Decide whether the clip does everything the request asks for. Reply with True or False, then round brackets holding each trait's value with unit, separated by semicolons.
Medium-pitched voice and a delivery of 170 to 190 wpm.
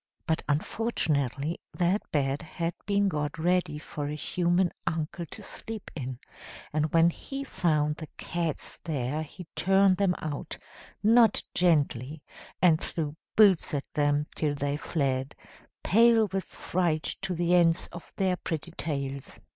False (165 Hz; 140 wpm)